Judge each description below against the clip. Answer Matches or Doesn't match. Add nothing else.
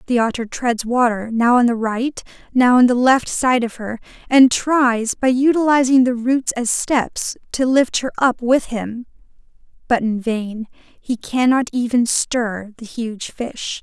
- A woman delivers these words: Matches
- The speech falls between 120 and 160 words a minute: Doesn't match